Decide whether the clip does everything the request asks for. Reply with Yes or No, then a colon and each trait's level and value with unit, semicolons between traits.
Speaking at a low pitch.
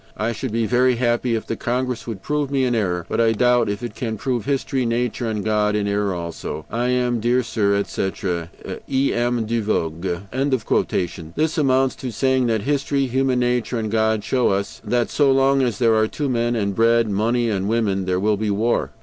Yes: low, 115 Hz